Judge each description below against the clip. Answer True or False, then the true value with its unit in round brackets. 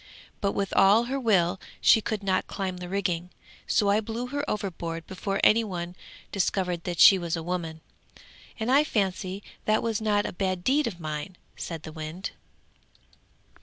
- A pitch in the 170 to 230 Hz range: True (190 Hz)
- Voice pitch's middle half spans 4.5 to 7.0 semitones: False (3.5 semitones)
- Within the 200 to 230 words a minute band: False (170 wpm)